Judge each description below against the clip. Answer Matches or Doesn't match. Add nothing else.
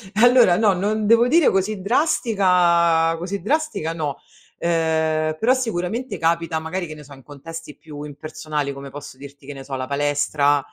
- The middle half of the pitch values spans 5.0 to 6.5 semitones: Matches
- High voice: Doesn't match